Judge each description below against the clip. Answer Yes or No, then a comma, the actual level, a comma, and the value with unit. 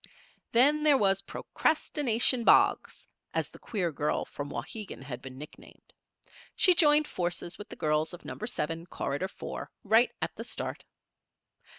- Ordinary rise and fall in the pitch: No, wide, 8.5 semitones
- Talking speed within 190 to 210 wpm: No, average, 150 wpm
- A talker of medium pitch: No, high, 195 Hz